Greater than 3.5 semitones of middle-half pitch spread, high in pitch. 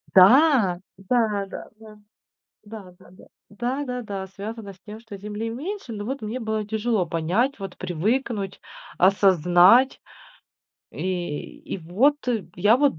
Yes: average, 4.1 semitones; high, 210 Hz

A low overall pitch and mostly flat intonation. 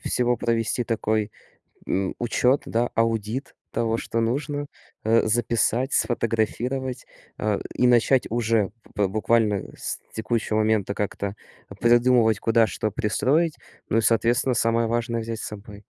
Yes: low, 115 Hz; narrow, 1.9 semitones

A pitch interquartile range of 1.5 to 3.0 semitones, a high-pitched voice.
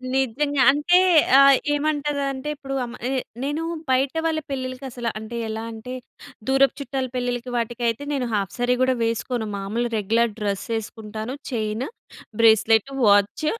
No: average, 3.6 semitones; high, 245 Hz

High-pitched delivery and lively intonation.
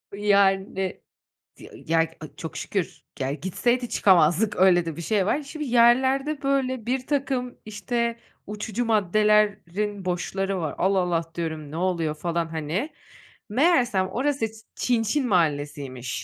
Yes: high, 200 Hz; wide, 6.2 semitones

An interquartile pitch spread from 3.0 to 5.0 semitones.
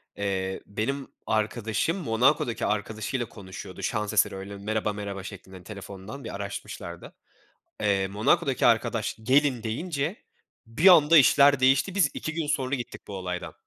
No: wide, 5.6 semitones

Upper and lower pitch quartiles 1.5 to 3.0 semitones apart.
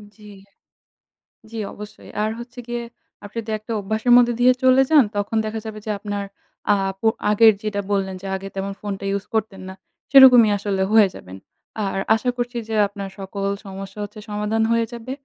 Yes: average, 2.7 semitones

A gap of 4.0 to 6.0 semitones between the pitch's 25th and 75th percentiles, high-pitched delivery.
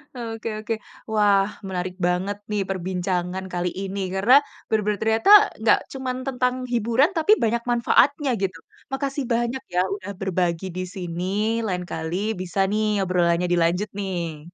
Yes: average, 4.4 semitones; high, 195 Hz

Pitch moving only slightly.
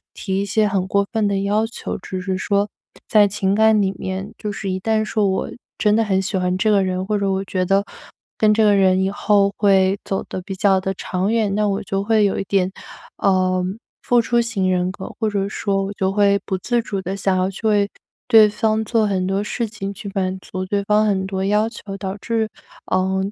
Yes: narrow, 1.9 semitones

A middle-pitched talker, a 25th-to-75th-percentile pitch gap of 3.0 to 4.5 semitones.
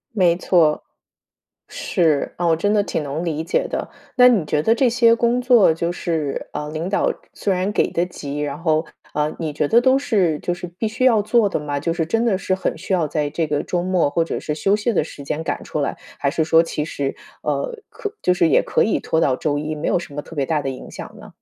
No: medium, 170 Hz; average, 5.1 semitones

